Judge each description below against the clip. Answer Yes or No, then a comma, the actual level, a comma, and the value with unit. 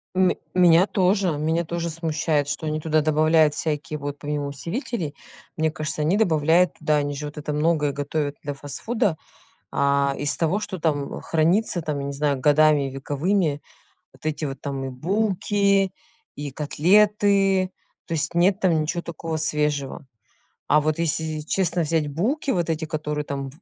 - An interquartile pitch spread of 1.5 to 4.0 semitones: Yes, average, 3.1 semitones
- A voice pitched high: No, medium, 155 Hz